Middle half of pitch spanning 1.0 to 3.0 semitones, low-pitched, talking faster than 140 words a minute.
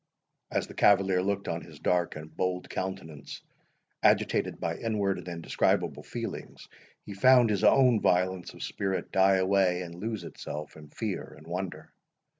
Yes: narrow, 2.5 semitones; very low, 95 Hz; average, 155 wpm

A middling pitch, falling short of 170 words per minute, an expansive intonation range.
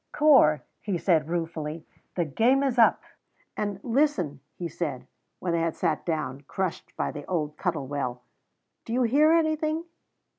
Yes: medium, 175 Hz; average, 155 wpm; wide, 8.6 semitones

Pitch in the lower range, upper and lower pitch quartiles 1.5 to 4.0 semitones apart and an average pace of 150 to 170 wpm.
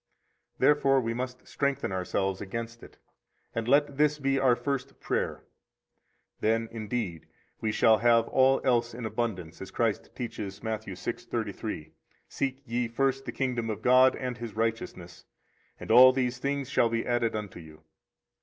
Yes: low, 120 Hz; average, 3.1 semitones; average, 160 wpm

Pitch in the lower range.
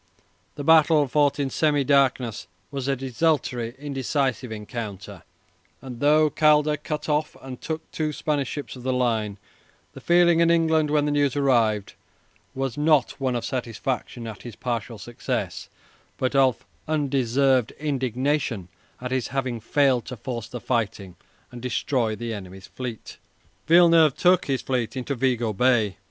Yes: low, 130 Hz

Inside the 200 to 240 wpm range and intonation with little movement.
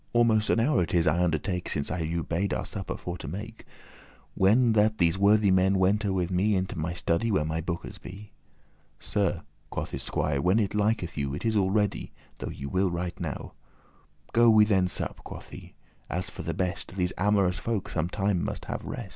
No: fast, 205 wpm; average, 3.4 semitones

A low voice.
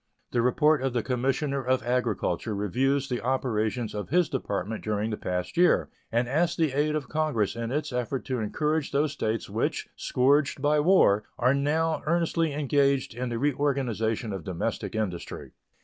Yes: low, 130 Hz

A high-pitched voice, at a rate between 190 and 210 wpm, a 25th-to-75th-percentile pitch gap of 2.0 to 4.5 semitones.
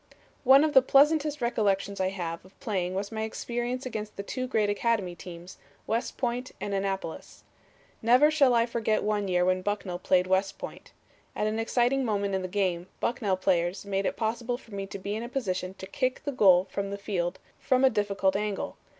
Yes: high, 205 Hz; average, 200 wpm; average, 4.1 semitones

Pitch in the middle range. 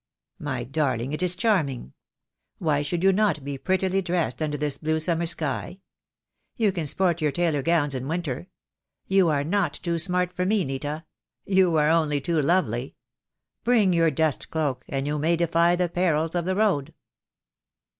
Yes: medium, 165 Hz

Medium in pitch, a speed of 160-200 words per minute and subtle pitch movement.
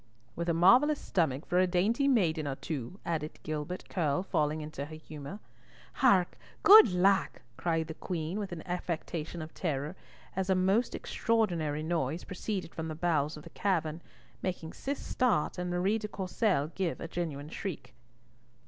No: medium, 175 Hz; average, 165 wpm; average, 3.6 semitones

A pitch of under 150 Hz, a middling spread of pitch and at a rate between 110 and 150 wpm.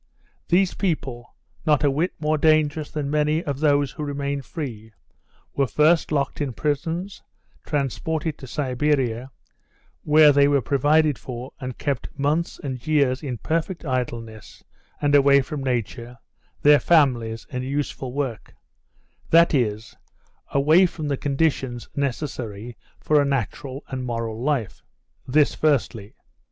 Yes: medium, 140 Hz; average, 3.2 semitones; slow, 135 wpm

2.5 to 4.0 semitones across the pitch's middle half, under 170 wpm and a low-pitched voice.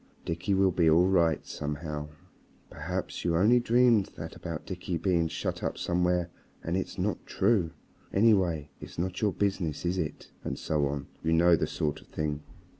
No: average, 3.1 semitones; average, 175 wpm; very low, 85 Hz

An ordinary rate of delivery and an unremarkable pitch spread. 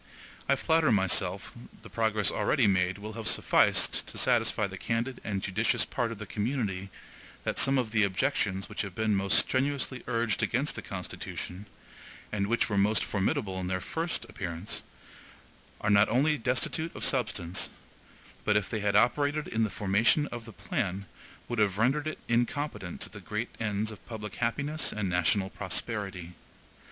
Yes: average, 165 wpm; average, 3.9 semitones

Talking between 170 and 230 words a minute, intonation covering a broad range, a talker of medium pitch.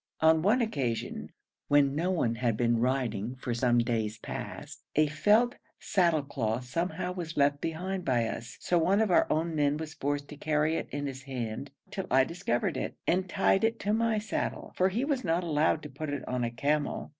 Yes: average, 200 wpm; wide, 5.9 semitones; medium, 150 Hz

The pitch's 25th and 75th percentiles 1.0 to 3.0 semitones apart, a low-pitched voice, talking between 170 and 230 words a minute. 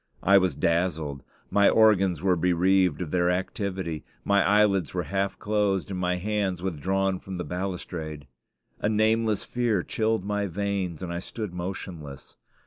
No: narrow, 2.4 semitones; very low, 95 Hz; average, 150 wpm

